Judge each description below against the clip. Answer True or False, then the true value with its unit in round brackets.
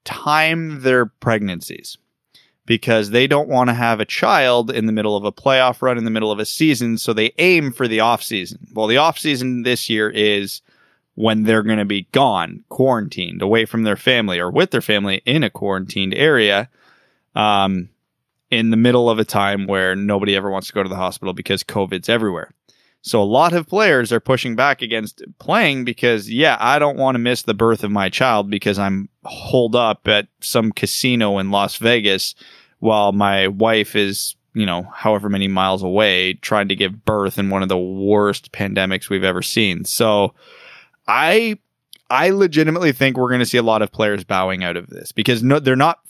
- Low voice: True (110 Hz)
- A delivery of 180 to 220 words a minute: True (200 wpm)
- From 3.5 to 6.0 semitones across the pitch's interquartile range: True (3.8 semitones)